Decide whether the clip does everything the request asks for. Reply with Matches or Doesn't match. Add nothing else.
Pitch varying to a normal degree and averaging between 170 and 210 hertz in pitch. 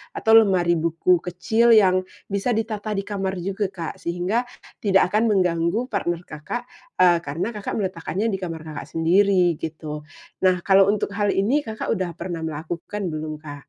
Matches